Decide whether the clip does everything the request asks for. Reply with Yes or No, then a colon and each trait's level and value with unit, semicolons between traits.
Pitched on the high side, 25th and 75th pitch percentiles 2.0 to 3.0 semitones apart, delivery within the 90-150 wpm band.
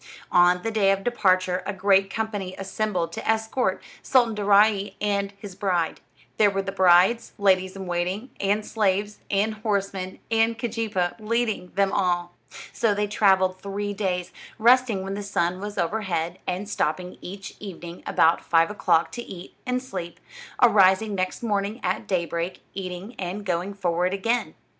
No: high, 195 Hz; narrow, 2.5 semitones; average, 160 wpm